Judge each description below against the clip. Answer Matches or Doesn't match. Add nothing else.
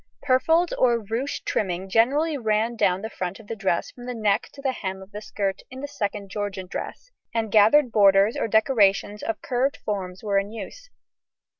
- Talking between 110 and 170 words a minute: Doesn't match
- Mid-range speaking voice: Doesn't match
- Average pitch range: Matches